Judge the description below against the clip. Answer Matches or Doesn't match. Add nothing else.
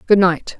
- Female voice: Matches